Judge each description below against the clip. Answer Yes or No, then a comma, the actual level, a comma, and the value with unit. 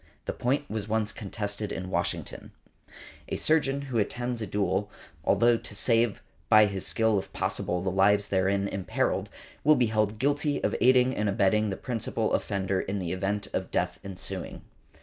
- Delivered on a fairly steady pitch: No, average, 3.3 semitones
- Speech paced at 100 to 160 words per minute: No, average, 170 wpm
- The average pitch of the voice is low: Yes, low, 105 Hz